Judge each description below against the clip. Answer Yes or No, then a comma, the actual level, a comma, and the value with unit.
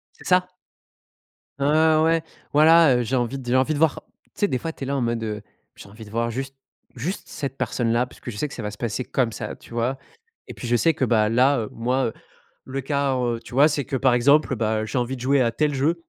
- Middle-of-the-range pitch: No, low, 130 Hz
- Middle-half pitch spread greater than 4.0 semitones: No, average, 3.5 semitones